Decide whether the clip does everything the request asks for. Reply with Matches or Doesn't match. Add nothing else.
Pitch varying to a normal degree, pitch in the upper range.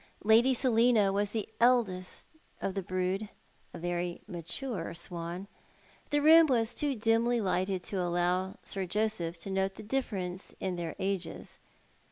Matches